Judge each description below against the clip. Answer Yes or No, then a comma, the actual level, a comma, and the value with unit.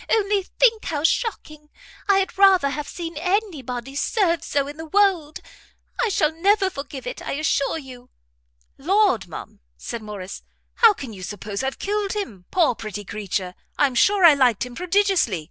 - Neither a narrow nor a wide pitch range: No, wide, 8.0 semitones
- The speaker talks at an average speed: Yes, average, 170 wpm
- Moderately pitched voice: No, very high, 305 Hz